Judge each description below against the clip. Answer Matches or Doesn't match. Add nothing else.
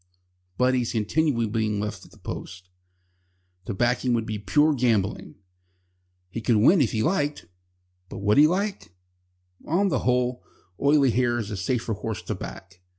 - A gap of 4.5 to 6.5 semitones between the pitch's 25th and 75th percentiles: Matches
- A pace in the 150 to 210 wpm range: Matches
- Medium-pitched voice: Doesn't match